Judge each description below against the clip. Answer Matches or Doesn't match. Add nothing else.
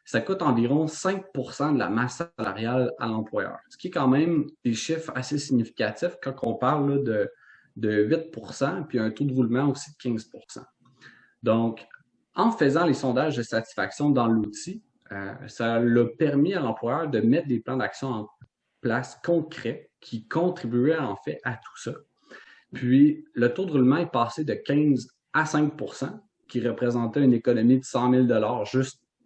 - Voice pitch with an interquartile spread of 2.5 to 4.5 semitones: Matches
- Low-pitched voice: Matches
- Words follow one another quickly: Doesn't match